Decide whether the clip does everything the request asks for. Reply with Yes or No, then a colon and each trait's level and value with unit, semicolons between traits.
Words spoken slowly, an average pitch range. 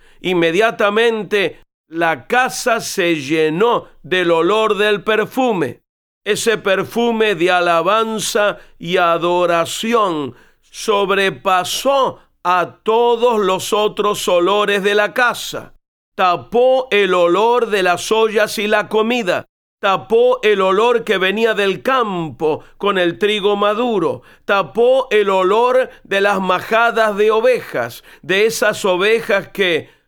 Yes: slow, 110 wpm; average, 3.8 semitones